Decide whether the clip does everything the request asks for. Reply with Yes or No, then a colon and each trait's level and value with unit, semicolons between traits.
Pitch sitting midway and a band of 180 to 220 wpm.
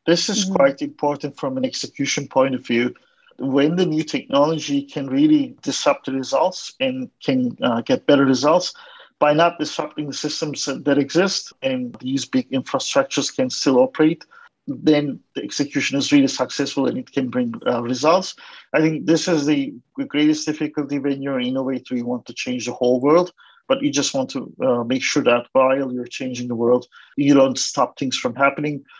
Yes: medium, 150 Hz; average, 185 wpm